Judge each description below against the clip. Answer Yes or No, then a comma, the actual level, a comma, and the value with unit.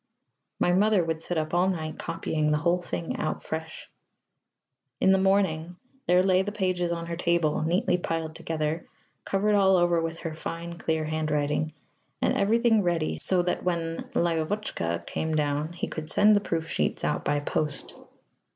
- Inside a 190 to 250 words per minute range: No, average, 170 wpm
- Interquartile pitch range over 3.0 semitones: No, average, 2.7 semitones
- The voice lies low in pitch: No, medium, 170 Hz